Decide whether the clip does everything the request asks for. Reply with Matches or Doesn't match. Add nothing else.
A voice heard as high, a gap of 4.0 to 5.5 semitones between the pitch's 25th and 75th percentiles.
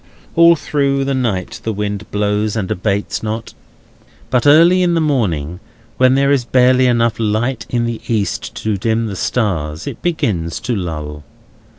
Doesn't match